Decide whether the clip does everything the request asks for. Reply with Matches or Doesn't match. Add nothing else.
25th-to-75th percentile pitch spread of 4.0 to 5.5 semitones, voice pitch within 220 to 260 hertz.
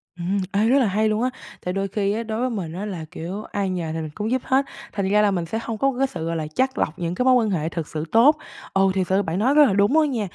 Doesn't match